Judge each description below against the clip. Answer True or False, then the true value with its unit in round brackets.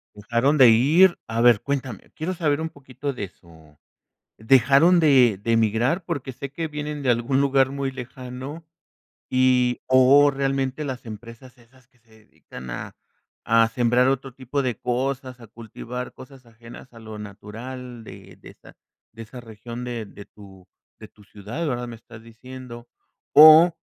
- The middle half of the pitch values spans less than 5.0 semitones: True (3.1 semitones)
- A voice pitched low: True (125 Hz)